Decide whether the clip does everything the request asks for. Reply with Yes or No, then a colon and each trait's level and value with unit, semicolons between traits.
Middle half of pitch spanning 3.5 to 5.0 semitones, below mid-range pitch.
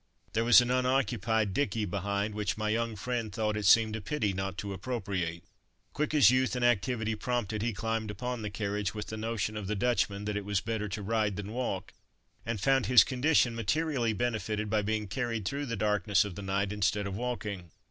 No: average, 3.0 semitones; low, 110 Hz